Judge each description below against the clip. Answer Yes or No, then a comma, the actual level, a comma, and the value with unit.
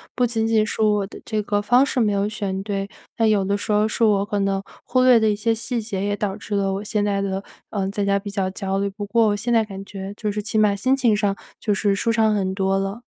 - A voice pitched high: Yes, high, 205 Hz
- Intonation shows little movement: Yes, narrow, 1.9 semitones